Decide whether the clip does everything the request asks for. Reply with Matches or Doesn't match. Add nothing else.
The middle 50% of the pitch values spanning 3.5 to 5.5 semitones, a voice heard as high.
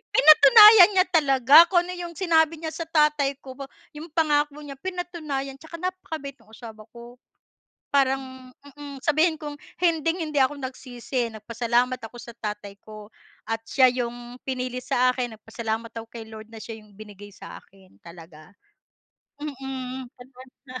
Matches